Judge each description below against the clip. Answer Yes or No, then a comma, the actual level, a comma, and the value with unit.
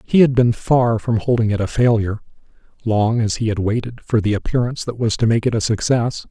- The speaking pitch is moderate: No, low, 115 Hz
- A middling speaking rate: No, fast, 220 wpm